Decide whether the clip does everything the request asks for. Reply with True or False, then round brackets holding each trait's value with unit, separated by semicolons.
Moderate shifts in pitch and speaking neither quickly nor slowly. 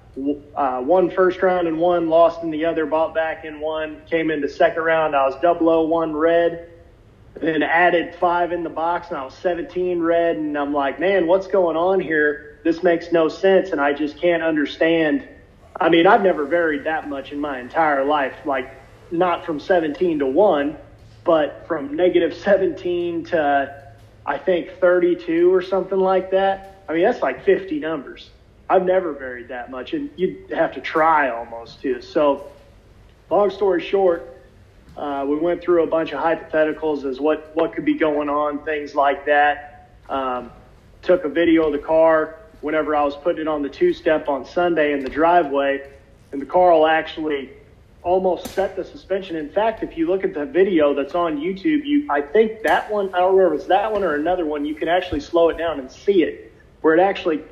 True (3.7 semitones; 195 wpm)